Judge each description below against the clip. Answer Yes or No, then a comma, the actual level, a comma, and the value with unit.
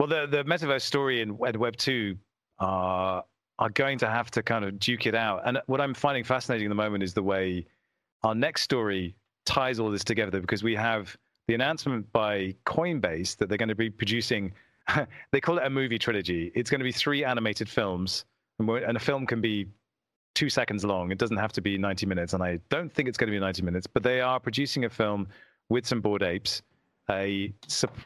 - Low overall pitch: Yes, low, 110 Hz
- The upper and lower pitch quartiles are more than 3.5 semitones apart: Yes, average, 4.1 semitones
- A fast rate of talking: Yes, fast, 220 wpm